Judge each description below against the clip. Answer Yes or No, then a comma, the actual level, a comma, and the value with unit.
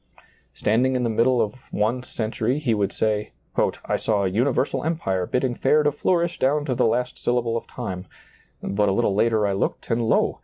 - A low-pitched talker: Yes, low, 115 Hz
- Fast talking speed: Yes, fast, 215 wpm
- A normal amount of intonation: Yes, average, 3.7 semitones